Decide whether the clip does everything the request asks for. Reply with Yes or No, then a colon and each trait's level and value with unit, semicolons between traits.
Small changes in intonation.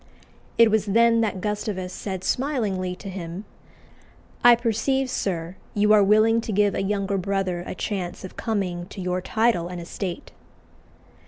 No: average, 3.3 semitones